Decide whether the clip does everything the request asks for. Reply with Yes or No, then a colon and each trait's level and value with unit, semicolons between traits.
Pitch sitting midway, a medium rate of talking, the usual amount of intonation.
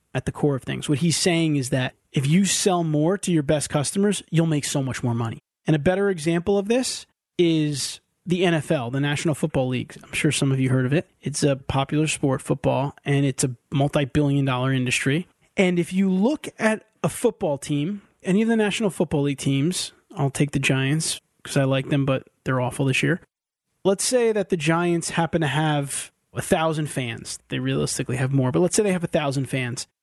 No: medium, 150 Hz; fast, 215 wpm; average, 4.6 semitones